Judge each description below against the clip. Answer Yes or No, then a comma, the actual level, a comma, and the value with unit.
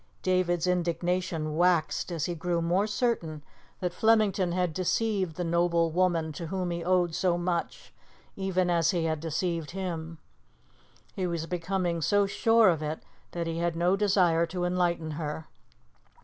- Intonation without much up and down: Yes, narrow, 1.9 semitones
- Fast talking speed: No, average, 155 wpm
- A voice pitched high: No, medium, 175 Hz